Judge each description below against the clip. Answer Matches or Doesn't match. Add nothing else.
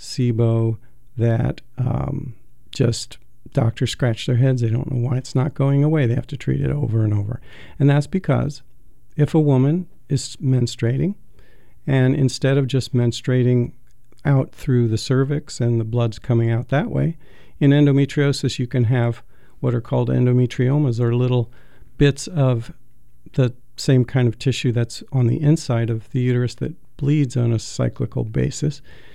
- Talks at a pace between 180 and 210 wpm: Doesn't match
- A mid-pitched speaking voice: Doesn't match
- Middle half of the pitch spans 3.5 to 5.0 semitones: Doesn't match